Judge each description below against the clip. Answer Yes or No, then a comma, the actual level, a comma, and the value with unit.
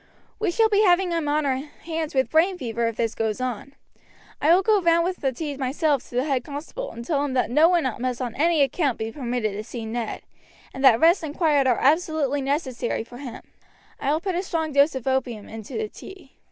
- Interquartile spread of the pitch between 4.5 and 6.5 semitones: Yes, average, 5.0 semitones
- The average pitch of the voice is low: No, very high, 280 Hz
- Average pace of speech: No, fast, 230 wpm